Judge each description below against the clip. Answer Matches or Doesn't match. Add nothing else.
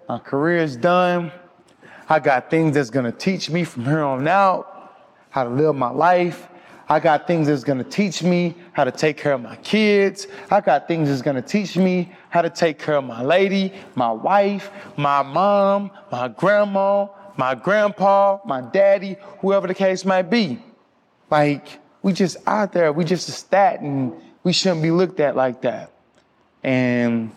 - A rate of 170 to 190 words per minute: Matches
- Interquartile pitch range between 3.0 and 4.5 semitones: Doesn't match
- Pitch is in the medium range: Matches